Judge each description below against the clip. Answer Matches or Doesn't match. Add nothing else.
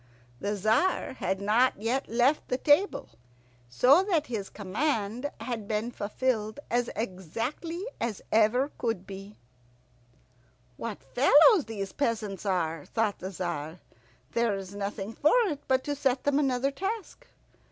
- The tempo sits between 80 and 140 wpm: Matches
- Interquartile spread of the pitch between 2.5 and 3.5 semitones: Doesn't match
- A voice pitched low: Doesn't match